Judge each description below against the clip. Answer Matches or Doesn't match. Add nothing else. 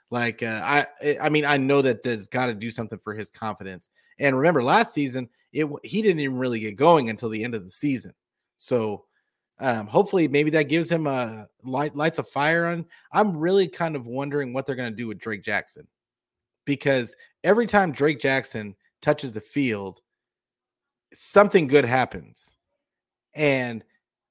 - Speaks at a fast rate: Doesn't match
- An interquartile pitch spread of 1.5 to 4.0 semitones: Doesn't match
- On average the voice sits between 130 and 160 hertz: Matches